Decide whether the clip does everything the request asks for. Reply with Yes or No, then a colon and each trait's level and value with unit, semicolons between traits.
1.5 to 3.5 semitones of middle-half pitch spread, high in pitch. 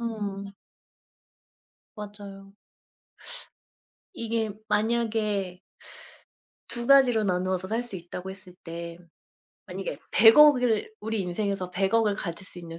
Yes: average, 3.2 semitones; high, 205 Hz